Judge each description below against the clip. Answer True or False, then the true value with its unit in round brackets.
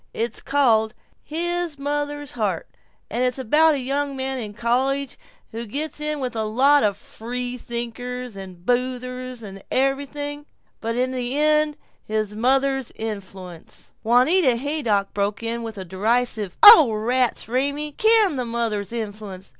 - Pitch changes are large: False (4.4 semitones)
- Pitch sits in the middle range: False (250 Hz)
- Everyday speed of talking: True (145 wpm)